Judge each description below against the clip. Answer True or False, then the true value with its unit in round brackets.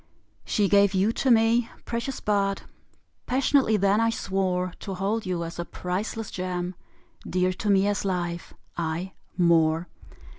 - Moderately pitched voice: False (195 Hz)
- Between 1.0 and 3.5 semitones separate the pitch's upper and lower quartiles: True (3.2 semitones)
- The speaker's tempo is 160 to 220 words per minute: False (145 wpm)